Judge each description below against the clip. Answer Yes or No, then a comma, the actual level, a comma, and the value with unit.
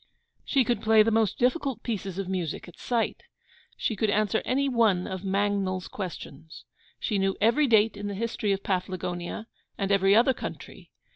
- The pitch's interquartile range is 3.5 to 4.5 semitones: No, average, 3.1 semitones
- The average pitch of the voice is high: Yes, high, 205 Hz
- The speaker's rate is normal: Yes, average, 170 wpm